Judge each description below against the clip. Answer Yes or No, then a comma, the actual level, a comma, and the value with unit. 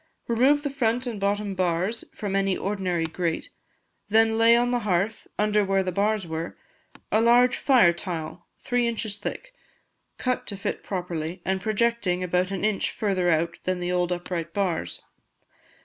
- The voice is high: Yes, high, 195 Hz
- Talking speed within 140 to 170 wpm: Yes, average, 165 wpm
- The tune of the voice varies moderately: Yes, average, 4.0 semitones